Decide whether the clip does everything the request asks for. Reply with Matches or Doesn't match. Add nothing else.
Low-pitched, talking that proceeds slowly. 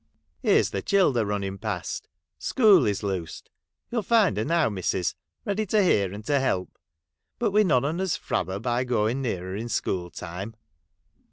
Doesn't match